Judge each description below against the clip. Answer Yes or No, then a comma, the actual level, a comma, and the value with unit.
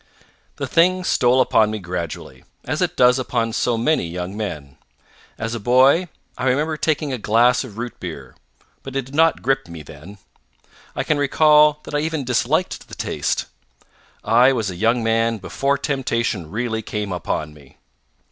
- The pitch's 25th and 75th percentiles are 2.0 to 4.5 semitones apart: No, average, 5.2 semitones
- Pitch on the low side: Yes, low, 120 Hz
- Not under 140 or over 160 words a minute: No, average, 170 wpm